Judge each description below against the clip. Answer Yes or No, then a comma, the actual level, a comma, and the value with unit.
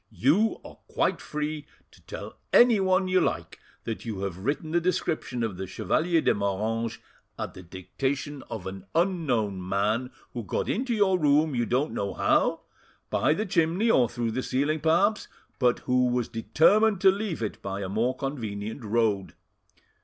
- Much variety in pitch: Yes, wide, 7.6 semitones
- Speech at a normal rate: Yes, average, 170 wpm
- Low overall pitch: Yes, low, 130 Hz